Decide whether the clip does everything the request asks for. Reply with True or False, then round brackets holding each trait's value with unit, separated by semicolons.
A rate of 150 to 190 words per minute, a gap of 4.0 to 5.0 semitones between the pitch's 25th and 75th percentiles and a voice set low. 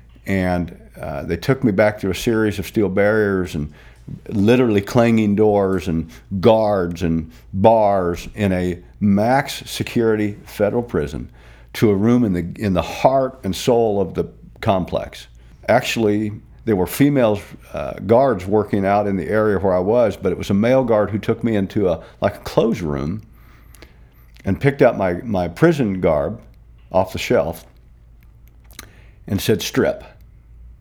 True (155 wpm; 4.7 semitones; 100 Hz)